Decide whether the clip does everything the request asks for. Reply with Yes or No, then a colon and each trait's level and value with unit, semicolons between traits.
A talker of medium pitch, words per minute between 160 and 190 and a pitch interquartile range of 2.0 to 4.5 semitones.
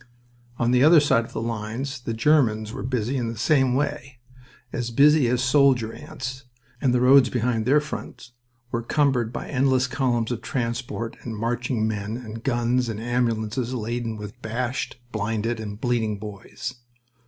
No: low, 120 Hz; average, 165 wpm; narrow, 2.4 semitones